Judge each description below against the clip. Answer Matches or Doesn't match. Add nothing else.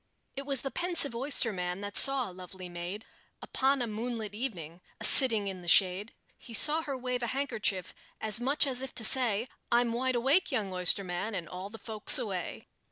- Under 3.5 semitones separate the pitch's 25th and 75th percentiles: Doesn't match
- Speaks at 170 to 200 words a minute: Matches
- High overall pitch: Matches